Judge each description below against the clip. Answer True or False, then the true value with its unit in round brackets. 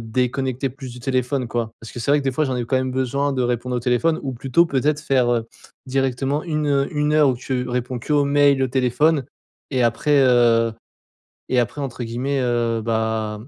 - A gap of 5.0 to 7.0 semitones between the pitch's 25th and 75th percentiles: False (2.6 semitones)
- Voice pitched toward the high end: False (130 Hz)